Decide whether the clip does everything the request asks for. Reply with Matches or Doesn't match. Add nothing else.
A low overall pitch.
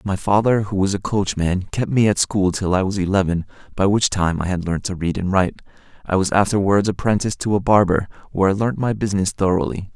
Matches